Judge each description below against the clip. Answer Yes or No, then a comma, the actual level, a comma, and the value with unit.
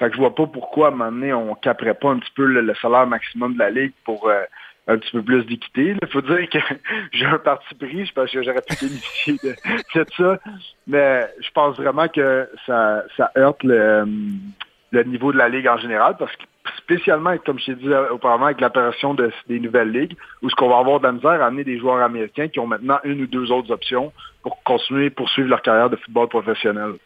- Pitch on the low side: Yes, low, 130 Hz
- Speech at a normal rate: No, fast, 245 wpm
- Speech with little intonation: No, average, 3.3 semitones